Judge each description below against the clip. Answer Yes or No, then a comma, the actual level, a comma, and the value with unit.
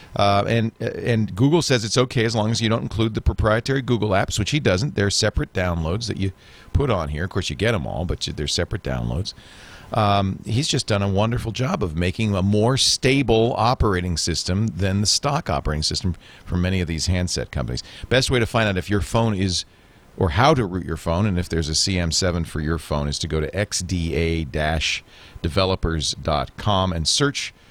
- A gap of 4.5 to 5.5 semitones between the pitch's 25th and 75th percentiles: Yes, average, 4.8 semitones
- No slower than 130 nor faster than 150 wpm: No, average, 200 wpm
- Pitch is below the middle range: Yes, low, 100 Hz